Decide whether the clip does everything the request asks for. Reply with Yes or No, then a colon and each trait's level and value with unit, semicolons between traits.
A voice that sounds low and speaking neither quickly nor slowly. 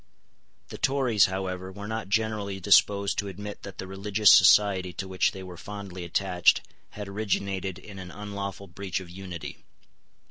Yes: low, 100 Hz; average, 155 wpm